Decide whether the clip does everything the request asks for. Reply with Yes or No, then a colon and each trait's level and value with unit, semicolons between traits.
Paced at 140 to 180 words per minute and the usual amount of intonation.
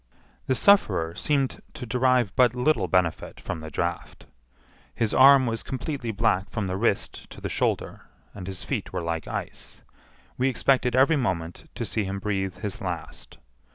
No: average, 165 wpm; wide, 5.7 semitones